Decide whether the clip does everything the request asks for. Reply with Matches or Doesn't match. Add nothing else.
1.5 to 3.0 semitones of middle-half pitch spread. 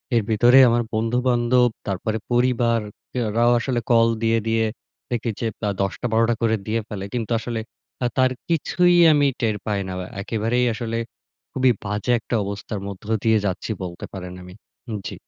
Matches